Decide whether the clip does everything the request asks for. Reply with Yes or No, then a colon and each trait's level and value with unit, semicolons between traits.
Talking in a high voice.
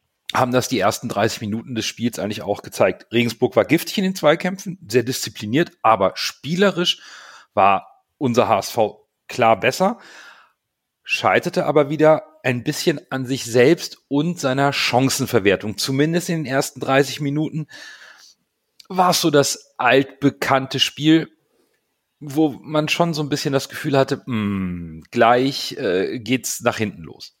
No: low, 135 Hz